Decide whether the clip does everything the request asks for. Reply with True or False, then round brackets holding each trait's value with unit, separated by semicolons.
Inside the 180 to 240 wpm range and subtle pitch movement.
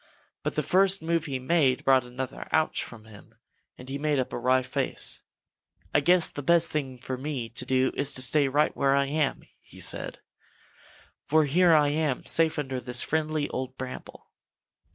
False (185 wpm; 3.2 semitones)